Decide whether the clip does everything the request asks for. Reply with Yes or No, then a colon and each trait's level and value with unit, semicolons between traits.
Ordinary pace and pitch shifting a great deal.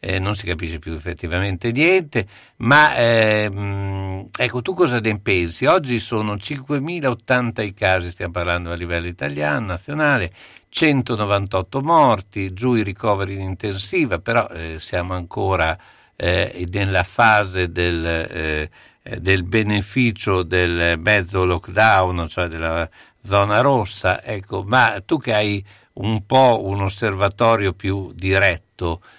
No: average, 125 wpm; average, 3.9 semitones